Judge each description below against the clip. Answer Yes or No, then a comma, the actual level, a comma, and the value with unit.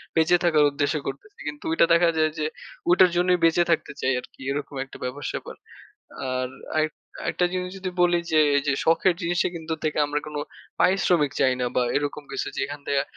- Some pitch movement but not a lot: Yes, average, 3.5 semitones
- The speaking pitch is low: No, medium, 155 Hz